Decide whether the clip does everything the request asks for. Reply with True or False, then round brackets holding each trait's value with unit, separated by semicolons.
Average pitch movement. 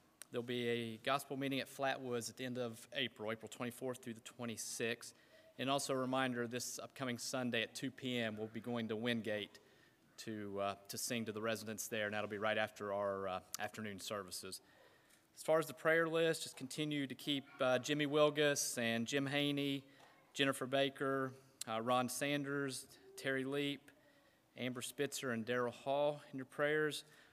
True (3.4 semitones)